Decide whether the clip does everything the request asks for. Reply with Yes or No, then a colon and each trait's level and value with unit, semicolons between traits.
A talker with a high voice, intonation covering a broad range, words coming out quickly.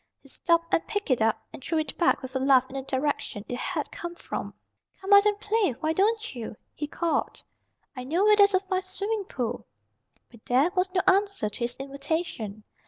Yes: very high, 320 Hz; wide, 7.0 semitones; fast, 210 wpm